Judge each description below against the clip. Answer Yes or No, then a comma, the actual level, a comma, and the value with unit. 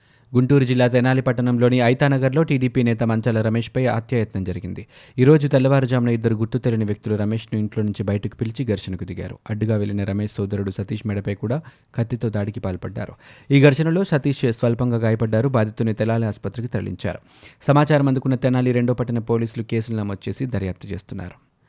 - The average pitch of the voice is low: Yes, low, 115 Hz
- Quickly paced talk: Yes, fast, 150 wpm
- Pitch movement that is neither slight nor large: Yes, average, 3.3 semitones